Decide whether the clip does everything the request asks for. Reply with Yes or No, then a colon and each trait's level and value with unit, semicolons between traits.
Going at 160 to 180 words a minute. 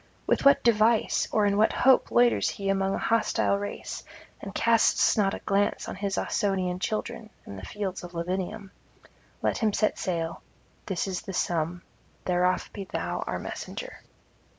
Yes: average, 165 wpm